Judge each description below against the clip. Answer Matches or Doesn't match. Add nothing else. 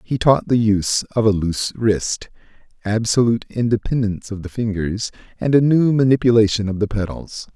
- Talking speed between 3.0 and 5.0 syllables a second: Doesn't match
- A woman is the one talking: Doesn't match